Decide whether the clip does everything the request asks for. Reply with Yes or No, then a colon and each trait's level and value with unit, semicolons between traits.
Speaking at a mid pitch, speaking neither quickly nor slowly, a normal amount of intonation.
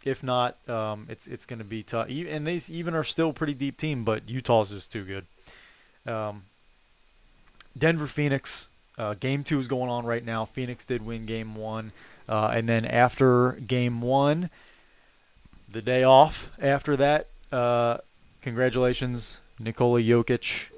No: low, 125 Hz; average, 155 wpm; average, 3.5 semitones